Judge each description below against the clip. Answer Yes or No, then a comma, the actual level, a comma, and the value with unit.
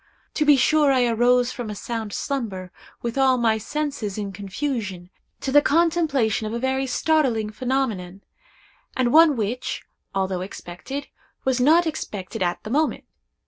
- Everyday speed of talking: Yes, average, 150 wpm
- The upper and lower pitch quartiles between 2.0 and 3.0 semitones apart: No, average, 5.1 semitones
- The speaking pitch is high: Yes, high, 245 Hz